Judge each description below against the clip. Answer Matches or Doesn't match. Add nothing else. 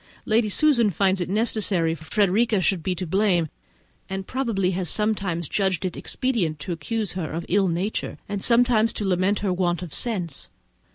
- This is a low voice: Doesn't match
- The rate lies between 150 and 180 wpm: Matches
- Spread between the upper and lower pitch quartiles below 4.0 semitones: Matches